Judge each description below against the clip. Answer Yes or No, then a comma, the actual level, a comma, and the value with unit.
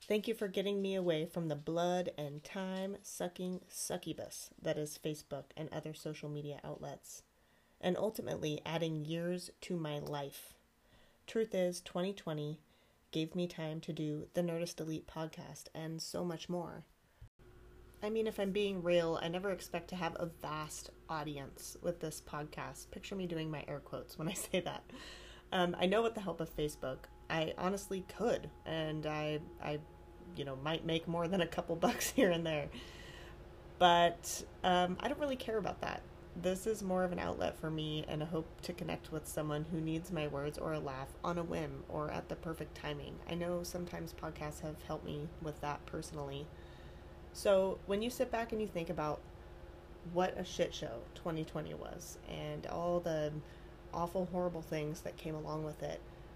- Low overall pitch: No, medium, 165 Hz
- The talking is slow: No, average, 180 wpm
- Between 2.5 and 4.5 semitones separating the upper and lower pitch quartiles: Yes, average, 2.9 semitones